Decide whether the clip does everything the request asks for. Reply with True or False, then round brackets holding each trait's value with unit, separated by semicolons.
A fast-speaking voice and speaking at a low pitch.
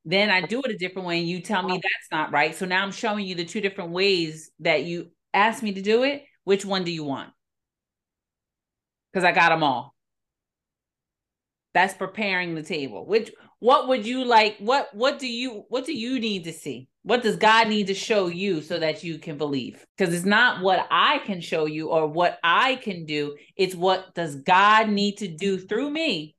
False (210 wpm; 190 Hz)